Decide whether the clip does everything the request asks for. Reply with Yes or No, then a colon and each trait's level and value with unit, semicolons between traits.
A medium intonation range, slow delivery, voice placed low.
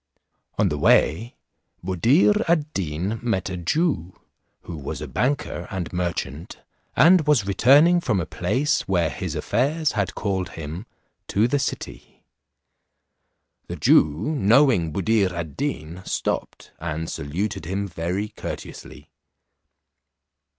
No: wide, 8.0 semitones; slow, 120 wpm; low, 100 Hz